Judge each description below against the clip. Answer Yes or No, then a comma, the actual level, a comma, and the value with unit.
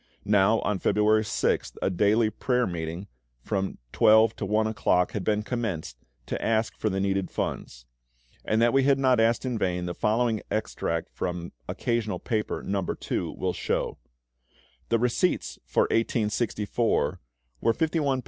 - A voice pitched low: Yes, low, 110 Hz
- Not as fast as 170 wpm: Yes, average, 150 wpm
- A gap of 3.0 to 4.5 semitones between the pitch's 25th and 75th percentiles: Yes, average, 3.3 semitones